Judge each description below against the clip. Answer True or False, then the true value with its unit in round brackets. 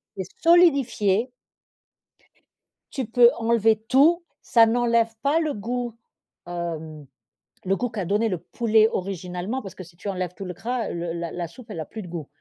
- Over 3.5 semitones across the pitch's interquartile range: True (5.2 semitones)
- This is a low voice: False (215 Hz)